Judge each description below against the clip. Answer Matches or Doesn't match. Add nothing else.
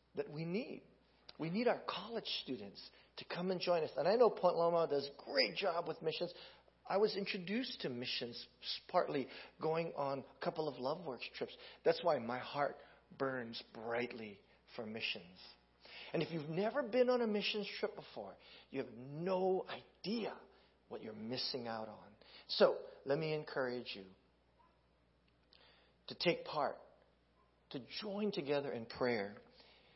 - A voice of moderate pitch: Matches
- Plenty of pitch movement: Matches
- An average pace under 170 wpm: Matches